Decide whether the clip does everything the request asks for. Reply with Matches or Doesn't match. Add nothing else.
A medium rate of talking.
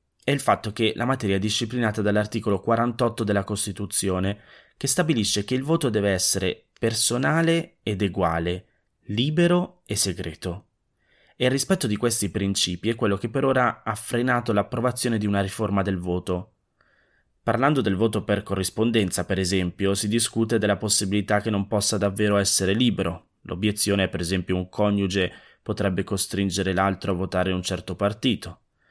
Matches